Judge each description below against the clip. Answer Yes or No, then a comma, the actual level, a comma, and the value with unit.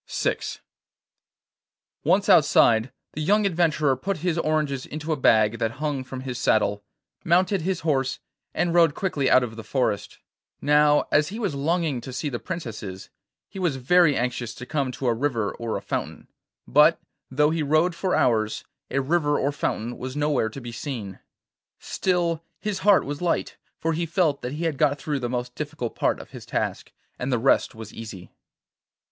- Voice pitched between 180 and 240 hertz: No, medium, 145 Hz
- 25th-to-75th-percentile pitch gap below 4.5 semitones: No, average, 5.1 semitones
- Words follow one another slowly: No, average, 180 wpm